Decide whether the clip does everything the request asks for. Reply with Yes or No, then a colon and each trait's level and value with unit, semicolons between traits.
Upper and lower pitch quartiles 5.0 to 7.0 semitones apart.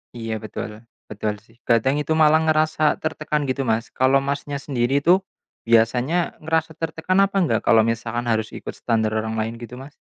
Yes: wide, 5.5 semitones